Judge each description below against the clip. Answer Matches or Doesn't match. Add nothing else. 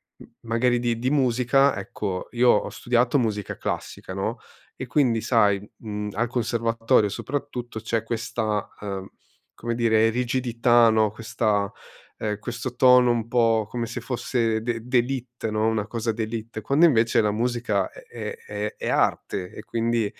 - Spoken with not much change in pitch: Matches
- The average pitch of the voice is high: Doesn't match